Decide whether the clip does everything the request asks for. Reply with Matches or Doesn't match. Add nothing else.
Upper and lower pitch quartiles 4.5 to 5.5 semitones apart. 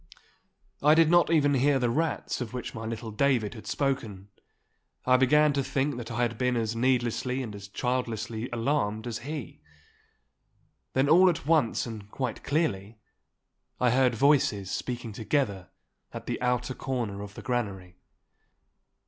Doesn't match